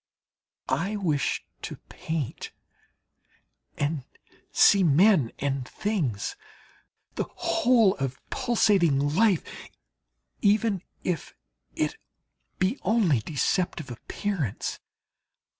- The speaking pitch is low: No, medium, 175 Hz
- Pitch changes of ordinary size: No, wide, 6.6 semitones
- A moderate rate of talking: No, slow, 80 wpm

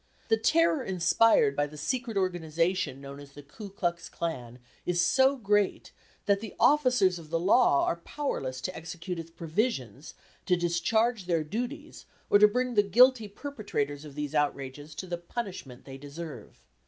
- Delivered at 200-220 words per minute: No, average, 165 wpm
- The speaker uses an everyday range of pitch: No, wide, 6.7 semitones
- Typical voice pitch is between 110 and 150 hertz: No, medium, 175 Hz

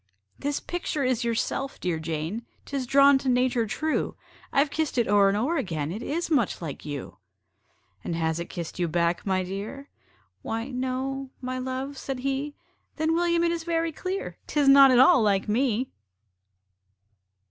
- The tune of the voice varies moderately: No, wide, 6.0 semitones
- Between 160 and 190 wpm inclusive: Yes, average, 170 wpm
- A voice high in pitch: Yes, very high, 255 Hz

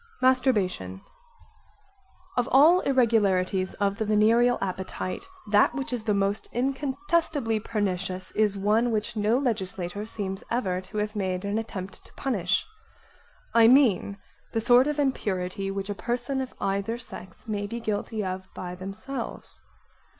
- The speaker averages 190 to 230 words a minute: No, average, 140 wpm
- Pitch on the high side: Yes, high, 215 Hz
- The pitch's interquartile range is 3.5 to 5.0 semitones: Yes, average, 4.0 semitones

